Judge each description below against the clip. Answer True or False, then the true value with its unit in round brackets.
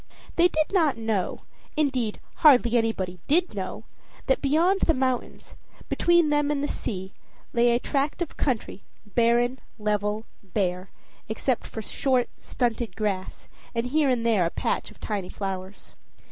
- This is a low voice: False (240 Hz)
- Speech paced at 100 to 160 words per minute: True (145 wpm)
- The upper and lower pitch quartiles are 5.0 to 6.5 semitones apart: True (5.5 semitones)